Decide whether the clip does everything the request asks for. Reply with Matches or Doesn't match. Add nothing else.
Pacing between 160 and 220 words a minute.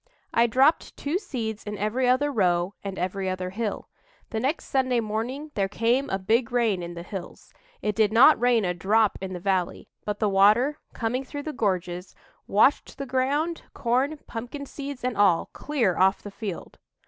Matches